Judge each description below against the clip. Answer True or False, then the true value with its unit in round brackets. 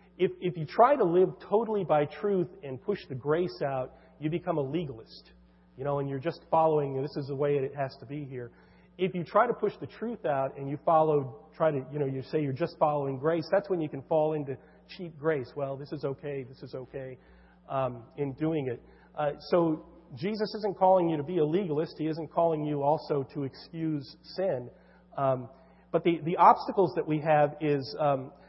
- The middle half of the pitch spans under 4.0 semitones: True (3.6 semitones)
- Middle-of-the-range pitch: True (155 Hz)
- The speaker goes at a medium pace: False (215 wpm)